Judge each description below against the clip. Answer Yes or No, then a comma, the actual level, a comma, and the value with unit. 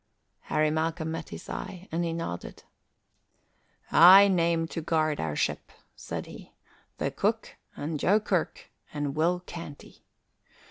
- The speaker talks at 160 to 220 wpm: No, slow, 135 wpm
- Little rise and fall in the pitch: Yes, narrow, 2.1 semitones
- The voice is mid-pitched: Yes, medium, 165 Hz